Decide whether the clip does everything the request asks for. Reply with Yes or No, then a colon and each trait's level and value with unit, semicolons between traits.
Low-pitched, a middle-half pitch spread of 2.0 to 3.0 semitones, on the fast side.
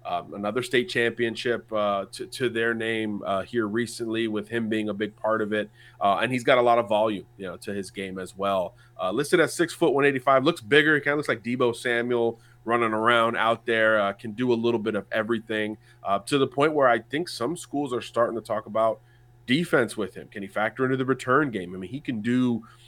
Yes: low, 115 Hz; narrow, 2.4 semitones; fast, 245 wpm